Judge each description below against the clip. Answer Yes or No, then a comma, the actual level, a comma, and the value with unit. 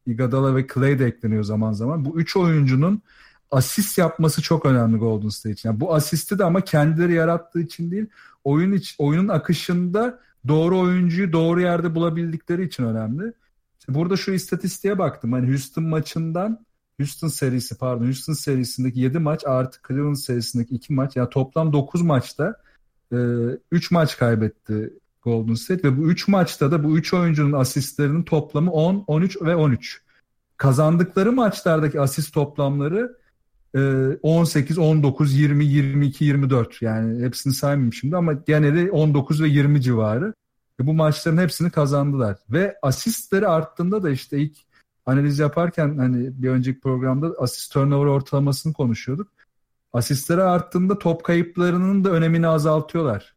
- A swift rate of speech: Yes, fast, 145 wpm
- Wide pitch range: No, average, 4.5 semitones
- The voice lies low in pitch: No, medium, 150 Hz